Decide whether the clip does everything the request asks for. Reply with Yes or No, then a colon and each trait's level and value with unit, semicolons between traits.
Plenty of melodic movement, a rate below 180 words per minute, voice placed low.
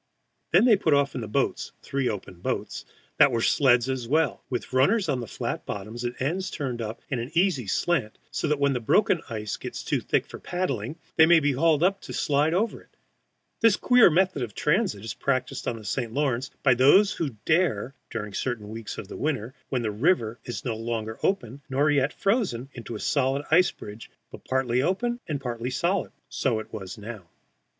No: wide, 5.7 semitones; fast, 205 wpm; low, 130 Hz